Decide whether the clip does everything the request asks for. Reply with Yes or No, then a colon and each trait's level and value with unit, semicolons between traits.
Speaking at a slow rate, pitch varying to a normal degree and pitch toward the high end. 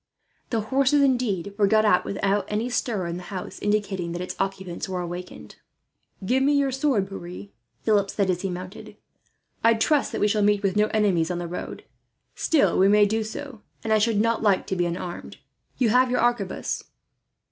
No: average, 195 wpm; average, 3.8 semitones; high, 205 Hz